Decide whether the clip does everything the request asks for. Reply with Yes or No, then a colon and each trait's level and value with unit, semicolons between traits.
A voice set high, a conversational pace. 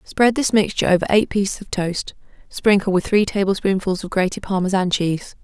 Yes: high, 195 Hz; average, 175 wpm